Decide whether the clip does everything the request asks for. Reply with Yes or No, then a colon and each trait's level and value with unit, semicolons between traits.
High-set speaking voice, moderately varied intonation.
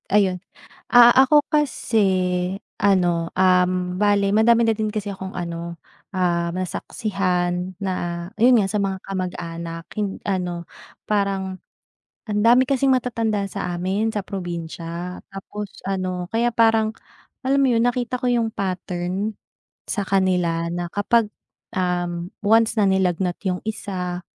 Yes: high, 195 Hz; average, 3.6 semitones